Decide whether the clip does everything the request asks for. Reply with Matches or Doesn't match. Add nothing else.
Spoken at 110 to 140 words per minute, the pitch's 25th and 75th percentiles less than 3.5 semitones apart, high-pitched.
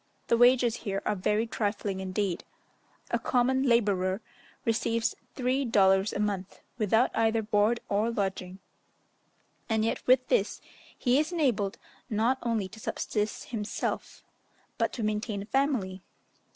Matches